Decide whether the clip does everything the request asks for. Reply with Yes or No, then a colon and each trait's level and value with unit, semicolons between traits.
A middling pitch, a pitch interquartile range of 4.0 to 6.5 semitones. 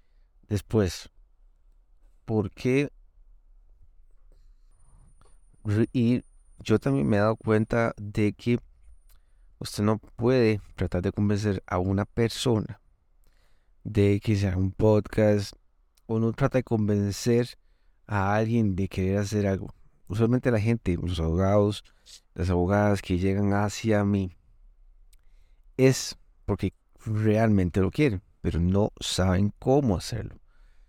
No: low, 100 Hz; average, 4.5 semitones